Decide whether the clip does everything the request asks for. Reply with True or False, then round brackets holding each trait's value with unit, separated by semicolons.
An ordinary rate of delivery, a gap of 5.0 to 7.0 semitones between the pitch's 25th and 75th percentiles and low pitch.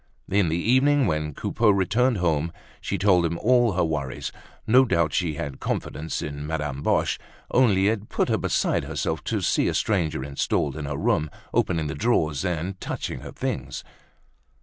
True (170 wpm; 5.5 semitones; 85 Hz)